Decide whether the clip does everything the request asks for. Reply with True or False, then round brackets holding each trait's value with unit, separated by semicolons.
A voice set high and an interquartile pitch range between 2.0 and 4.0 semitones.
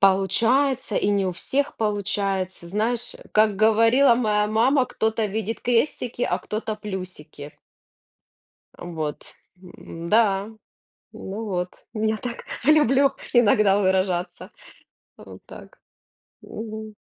True (215 Hz; 3.2 semitones)